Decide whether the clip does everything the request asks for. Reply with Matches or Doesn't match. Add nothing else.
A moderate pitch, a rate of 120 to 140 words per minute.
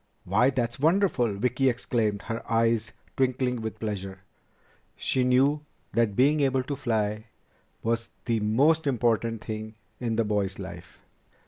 Doesn't match